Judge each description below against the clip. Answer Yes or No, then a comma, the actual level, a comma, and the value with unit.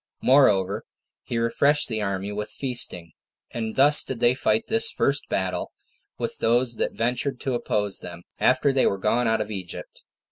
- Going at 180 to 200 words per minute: No, average, 170 wpm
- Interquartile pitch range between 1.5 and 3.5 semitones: No, average, 4.6 semitones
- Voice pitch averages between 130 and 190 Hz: No, low, 115 Hz